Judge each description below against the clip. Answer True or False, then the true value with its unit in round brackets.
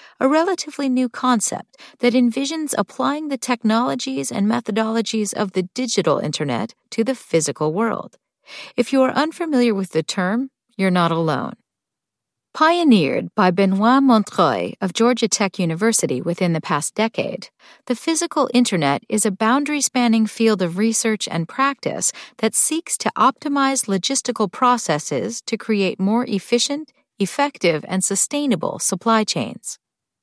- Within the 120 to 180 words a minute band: True (135 wpm)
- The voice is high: True (225 Hz)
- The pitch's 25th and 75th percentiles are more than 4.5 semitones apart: True (5.2 semitones)